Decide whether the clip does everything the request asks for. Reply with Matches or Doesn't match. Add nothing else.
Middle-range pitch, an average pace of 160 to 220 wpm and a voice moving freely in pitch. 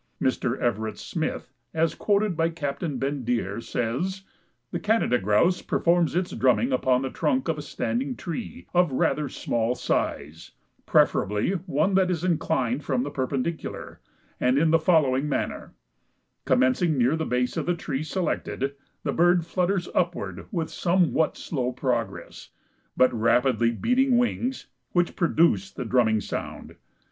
Doesn't match